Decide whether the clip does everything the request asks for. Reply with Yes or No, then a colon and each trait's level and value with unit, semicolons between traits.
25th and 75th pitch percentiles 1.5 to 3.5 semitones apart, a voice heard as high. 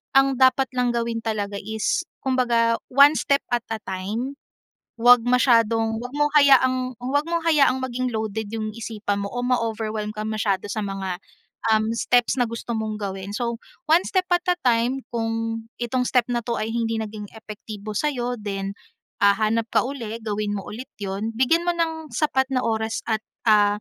Yes: average, 3.0 semitones; high, 230 Hz